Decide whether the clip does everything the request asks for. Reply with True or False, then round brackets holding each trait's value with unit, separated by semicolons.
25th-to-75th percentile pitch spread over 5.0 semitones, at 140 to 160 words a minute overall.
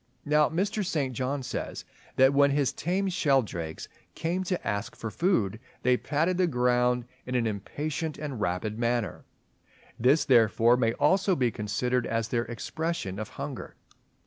True (5.4 semitones; 150 wpm)